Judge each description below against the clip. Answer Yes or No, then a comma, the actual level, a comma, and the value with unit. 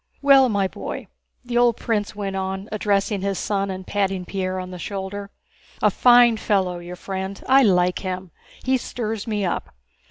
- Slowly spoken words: No, average, 160 wpm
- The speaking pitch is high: Yes, high, 200 Hz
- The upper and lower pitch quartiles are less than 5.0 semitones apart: Yes, narrow, 2.6 semitones